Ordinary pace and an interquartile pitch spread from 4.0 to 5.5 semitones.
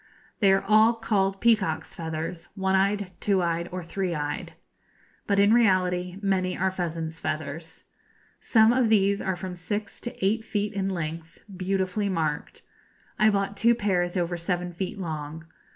No: average, 155 wpm; average, 2.9 semitones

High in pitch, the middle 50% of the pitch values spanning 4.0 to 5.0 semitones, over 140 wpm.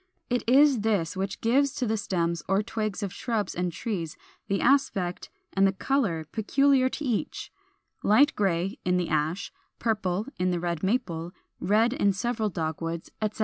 Yes: high, 200 Hz; average, 4.7 semitones; average, 165 wpm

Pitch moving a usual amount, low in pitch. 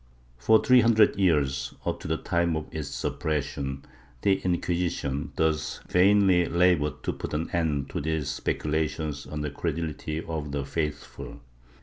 Yes: average, 3.0 semitones; very low, 80 Hz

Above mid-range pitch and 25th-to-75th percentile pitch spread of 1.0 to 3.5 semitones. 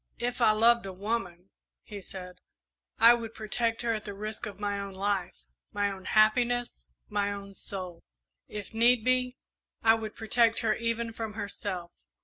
Yes: high, 215 Hz; narrow, 2.6 semitones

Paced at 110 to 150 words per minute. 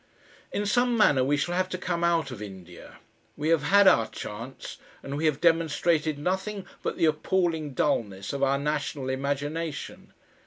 No: average, 165 wpm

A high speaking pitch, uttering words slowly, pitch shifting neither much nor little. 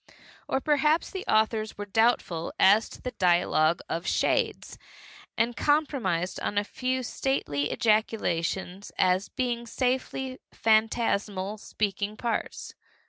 Yes: high, 215 Hz; slow, 115 wpm; average, 4.9 semitones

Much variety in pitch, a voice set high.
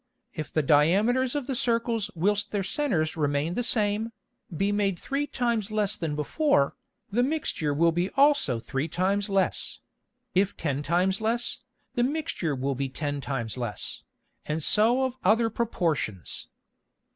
Yes: wide, 7.4 semitones; high, 195 Hz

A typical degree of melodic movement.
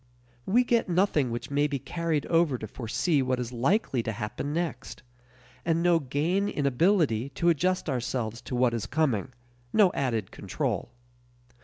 No: wide, 5.7 semitones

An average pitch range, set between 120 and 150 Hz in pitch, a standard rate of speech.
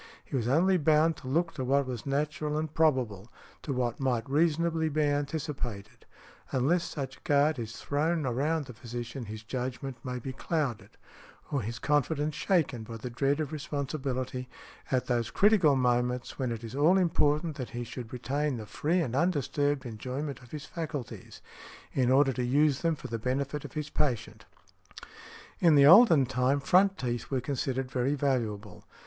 Yes: average, 3.5 semitones; low, 135 Hz; average, 170 wpm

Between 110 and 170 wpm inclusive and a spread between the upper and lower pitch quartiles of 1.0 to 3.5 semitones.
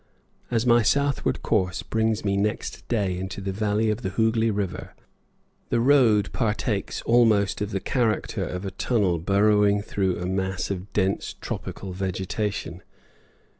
Yes: average, 145 wpm; average, 2.8 semitones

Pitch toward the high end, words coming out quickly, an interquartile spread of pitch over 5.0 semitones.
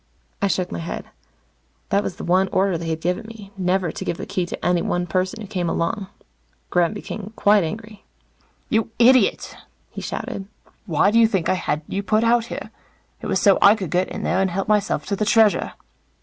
No: high, 195 Hz; fast, 210 wpm; average, 3.1 semitones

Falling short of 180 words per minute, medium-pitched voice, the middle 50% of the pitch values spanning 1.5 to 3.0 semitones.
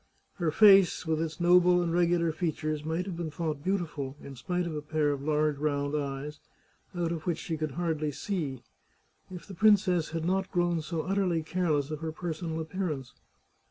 No: average, 190 wpm; medium, 165 Hz; narrow, 2.6 semitones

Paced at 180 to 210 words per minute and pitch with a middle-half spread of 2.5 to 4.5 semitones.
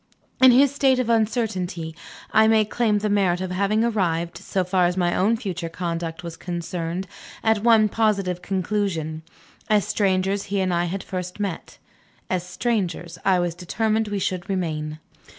No: average, 165 wpm; average, 3.5 semitones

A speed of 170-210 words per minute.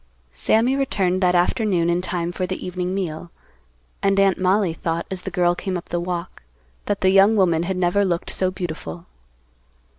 Yes: average, 180 wpm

